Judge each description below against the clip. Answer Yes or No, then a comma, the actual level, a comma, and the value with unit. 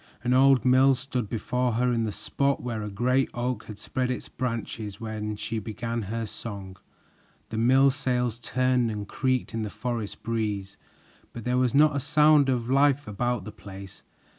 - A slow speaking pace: No, average, 180 wpm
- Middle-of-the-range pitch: No, low, 120 Hz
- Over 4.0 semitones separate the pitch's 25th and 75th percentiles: No, average, 3.0 semitones